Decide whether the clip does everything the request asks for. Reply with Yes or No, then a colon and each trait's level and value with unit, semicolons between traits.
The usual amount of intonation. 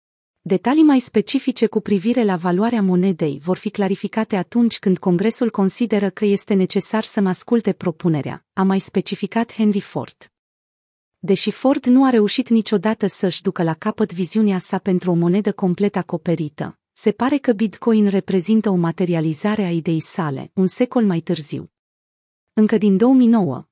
Yes: average, 3.3 semitones